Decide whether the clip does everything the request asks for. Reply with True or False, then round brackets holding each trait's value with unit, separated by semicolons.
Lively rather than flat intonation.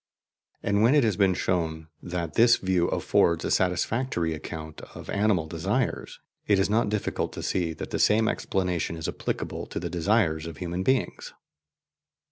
False (4.3 semitones)